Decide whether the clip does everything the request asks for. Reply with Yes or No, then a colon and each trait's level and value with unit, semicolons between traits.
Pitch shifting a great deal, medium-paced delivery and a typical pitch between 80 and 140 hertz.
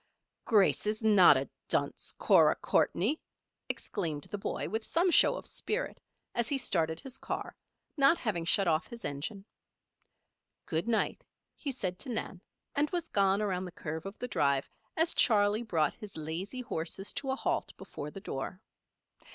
No: wide, 6.6 semitones; average, 165 wpm; high, 205 Hz